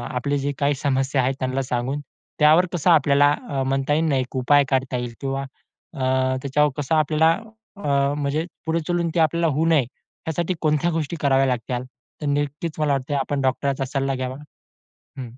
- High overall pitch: No, medium, 140 Hz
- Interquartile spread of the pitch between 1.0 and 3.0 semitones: Yes, narrow, 2.5 semitones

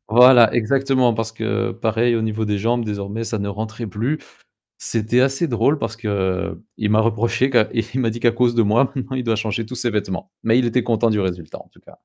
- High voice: No, low, 115 Hz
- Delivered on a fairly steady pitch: Yes, narrow, 2.2 semitones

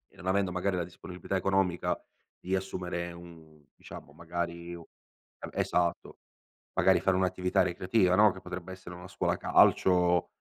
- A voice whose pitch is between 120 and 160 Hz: No, very low, 90 Hz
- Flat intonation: Yes, narrow, 1.4 semitones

